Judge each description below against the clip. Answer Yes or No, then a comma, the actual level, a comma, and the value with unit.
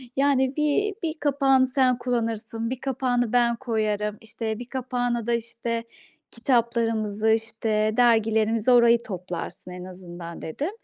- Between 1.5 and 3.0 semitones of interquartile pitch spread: Yes, average, 2.7 semitones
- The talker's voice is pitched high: Yes, high, 230 Hz